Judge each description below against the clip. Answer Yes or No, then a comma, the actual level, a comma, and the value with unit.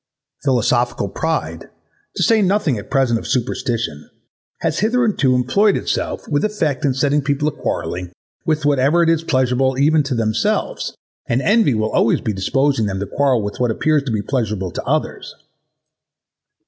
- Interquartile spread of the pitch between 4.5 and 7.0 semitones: Yes, average, 4.9 semitones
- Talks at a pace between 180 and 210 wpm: No, average, 160 wpm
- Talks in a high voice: No, low, 135 Hz